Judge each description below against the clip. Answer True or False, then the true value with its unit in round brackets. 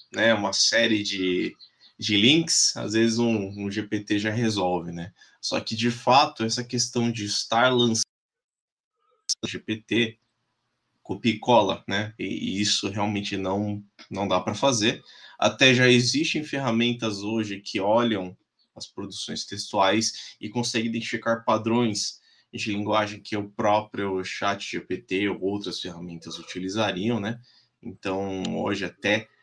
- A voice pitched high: False (110 Hz)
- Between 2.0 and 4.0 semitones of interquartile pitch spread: True (2.9 semitones)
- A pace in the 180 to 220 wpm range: False (135 wpm)